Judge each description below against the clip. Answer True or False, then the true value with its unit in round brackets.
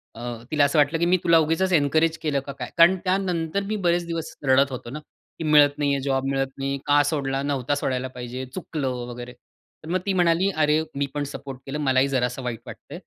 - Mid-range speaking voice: True (145 Hz)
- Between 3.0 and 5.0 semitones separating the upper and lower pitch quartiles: True (3.5 semitones)